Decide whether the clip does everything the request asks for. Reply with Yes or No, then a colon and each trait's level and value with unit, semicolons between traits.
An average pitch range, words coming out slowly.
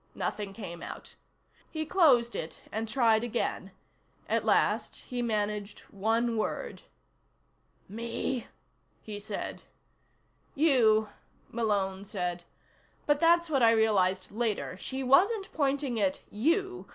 Yes: average, 4.8 semitones; slow, 115 wpm